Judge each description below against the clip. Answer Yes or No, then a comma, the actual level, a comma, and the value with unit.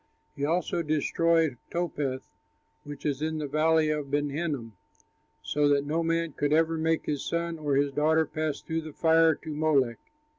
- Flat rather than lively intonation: Yes, narrow, 2.0 semitones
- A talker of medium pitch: Yes, medium, 155 Hz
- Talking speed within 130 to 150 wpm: No, average, 175 wpm